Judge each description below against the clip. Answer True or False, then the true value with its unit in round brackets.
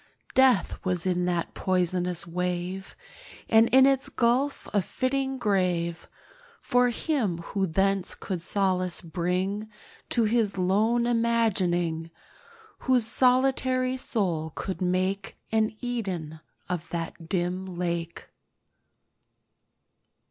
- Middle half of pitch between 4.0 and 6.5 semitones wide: True (4.9 semitones)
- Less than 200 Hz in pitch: True (190 Hz)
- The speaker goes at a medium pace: False (105 wpm)